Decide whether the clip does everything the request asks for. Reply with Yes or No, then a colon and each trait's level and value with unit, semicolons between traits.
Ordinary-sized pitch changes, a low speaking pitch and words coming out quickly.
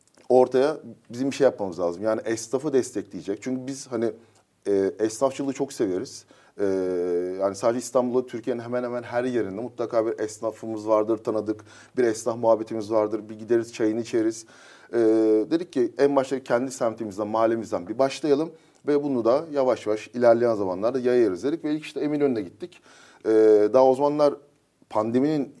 Yes: average, 3.6 semitones; low, 115 Hz; fast, 155 wpm